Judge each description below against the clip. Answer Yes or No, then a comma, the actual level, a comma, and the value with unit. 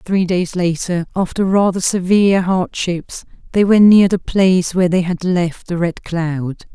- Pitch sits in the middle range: Yes, medium, 180 Hz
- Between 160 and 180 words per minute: Yes, average, 170 wpm